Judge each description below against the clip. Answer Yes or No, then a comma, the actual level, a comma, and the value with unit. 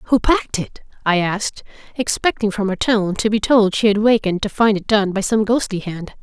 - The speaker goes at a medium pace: No, fast, 220 wpm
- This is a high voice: Yes, high, 210 Hz